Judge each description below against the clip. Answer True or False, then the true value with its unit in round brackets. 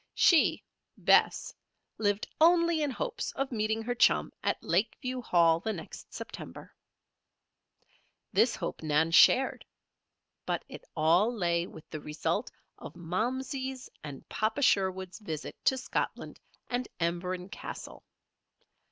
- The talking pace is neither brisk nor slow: False (120 wpm)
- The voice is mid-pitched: False (210 Hz)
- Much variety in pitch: True (7.1 semitones)